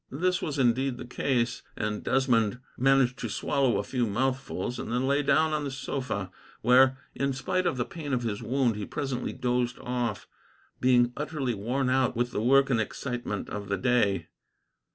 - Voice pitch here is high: No, low, 125 Hz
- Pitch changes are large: No, narrow, 2.4 semitones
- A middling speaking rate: Yes, average, 180 wpm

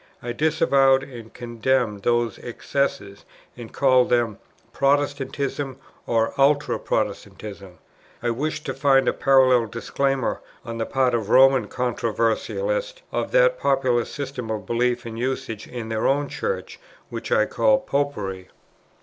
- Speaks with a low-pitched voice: Yes, low, 130 Hz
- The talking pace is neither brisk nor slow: No, slow, 130 wpm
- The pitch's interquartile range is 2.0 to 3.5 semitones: Yes, average, 3.1 semitones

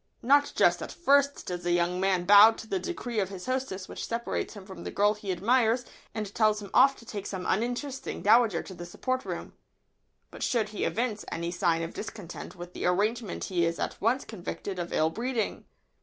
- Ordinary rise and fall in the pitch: Yes, average, 4.7 semitones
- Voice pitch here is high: Yes, high, 210 Hz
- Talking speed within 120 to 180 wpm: No, fast, 205 wpm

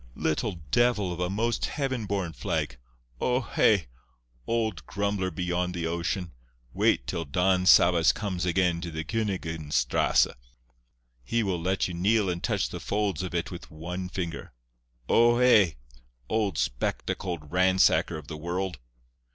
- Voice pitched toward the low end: Yes, very low, 90 Hz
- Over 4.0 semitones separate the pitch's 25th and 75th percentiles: No, average, 3.3 semitones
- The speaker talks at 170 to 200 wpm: No, average, 145 wpm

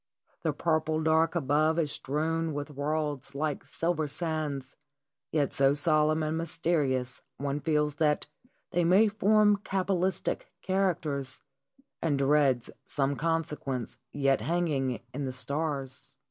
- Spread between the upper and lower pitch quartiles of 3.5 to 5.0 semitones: No, average, 2.8 semitones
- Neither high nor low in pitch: Yes, medium, 150 Hz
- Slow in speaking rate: Yes, slow, 120 wpm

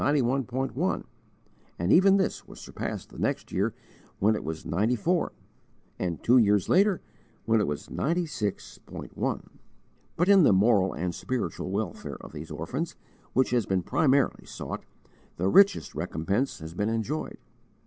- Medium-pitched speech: No, low, 115 Hz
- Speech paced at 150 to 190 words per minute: No, average, 140 wpm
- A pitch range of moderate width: No, wide, 7.3 semitones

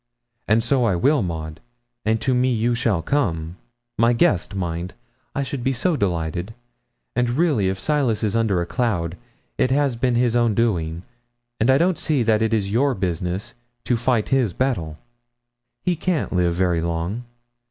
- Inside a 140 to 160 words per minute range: No, average, 175 wpm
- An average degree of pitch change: No, wide, 6.1 semitones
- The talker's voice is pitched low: Yes, low, 115 Hz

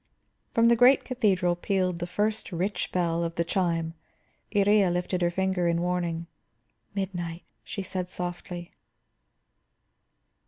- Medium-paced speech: No, slow, 125 wpm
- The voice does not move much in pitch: Yes, narrow, 2.3 semitones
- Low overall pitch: No, medium, 180 Hz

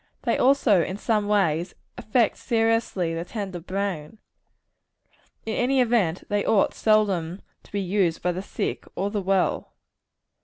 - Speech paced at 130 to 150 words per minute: Yes, average, 145 wpm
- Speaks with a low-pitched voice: No, high, 200 Hz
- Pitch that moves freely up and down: No, average, 3.6 semitones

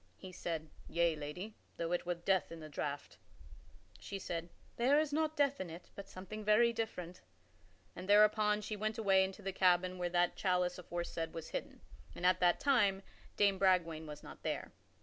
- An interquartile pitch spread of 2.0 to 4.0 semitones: Yes, average, 3.5 semitones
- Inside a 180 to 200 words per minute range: Yes, average, 185 wpm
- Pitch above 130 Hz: Yes, medium, 185 Hz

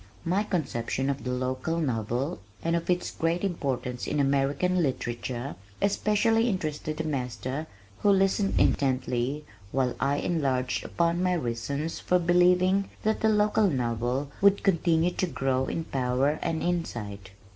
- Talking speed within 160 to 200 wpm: No, average, 140 wpm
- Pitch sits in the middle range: Yes, medium, 150 Hz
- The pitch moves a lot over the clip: Yes, wide, 5.7 semitones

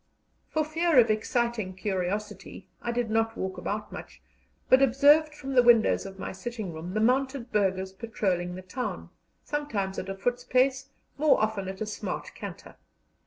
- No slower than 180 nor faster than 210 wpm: No, average, 165 wpm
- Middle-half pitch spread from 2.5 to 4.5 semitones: No, average, 5.1 semitones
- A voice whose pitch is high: Yes, high, 220 Hz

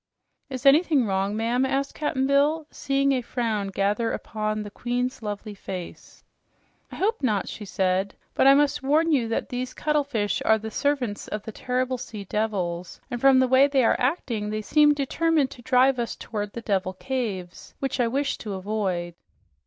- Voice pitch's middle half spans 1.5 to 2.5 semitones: No, average, 4.7 semitones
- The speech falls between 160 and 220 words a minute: Yes, average, 180 wpm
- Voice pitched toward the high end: Yes, high, 240 Hz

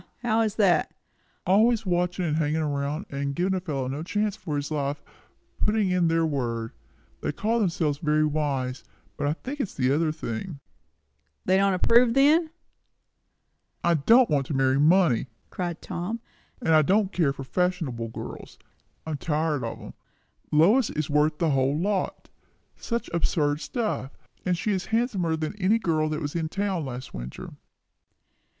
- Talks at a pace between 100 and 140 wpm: No, average, 170 wpm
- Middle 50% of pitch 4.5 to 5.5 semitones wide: Yes, average, 5.2 semitones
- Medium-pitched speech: Yes, medium, 165 Hz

